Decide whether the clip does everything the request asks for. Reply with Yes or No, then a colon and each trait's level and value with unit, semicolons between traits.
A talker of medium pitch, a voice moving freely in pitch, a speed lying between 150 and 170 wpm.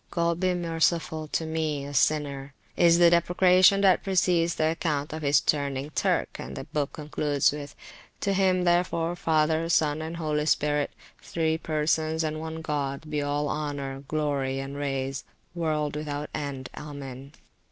No: medium, 155 Hz; narrow, 2.5 semitones; average, 160 wpm